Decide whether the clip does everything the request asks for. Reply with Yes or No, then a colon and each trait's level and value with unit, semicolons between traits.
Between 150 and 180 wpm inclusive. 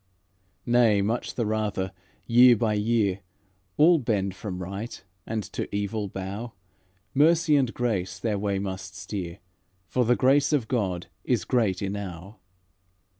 No: slow, 135 wpm